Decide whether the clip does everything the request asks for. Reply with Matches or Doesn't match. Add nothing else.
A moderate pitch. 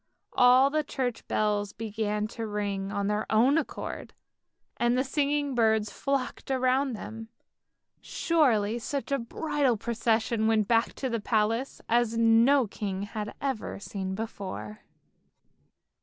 Doesn't match